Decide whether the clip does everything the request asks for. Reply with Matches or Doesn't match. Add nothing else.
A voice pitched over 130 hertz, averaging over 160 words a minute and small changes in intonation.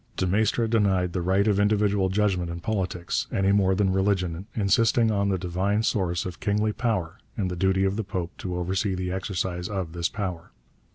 Doesn't match